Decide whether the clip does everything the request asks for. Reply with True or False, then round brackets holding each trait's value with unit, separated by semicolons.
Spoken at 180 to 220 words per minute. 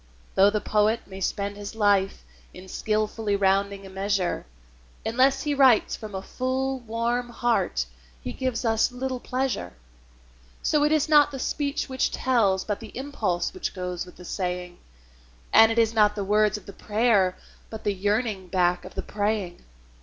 False (170 wpm)